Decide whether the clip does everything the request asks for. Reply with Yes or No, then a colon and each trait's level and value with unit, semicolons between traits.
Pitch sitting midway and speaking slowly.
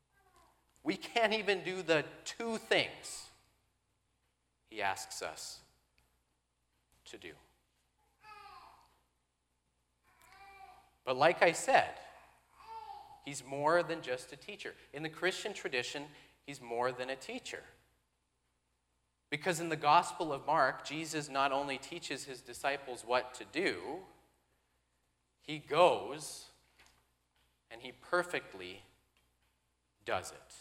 No: low, 125 Hz; slow, 105 wpm